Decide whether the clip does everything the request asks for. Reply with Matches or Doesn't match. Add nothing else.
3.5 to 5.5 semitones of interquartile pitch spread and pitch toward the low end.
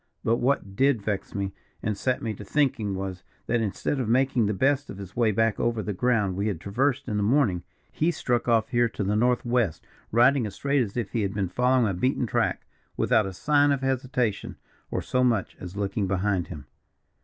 Matches